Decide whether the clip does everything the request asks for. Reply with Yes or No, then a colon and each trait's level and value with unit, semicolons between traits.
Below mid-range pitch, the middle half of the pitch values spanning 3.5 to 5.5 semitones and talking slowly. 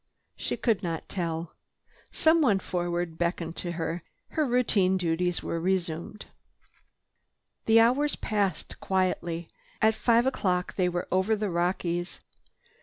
No: medium, 180 Hz; average, 3.8 semitones; slow, 115 wpm